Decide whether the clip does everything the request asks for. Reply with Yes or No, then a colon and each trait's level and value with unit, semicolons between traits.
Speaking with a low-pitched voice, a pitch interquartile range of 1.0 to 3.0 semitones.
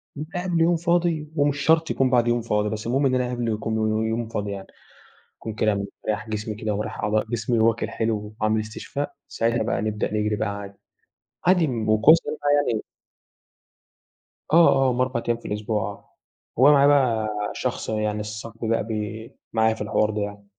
No: low, 110 Hz; average, 3.5 semitones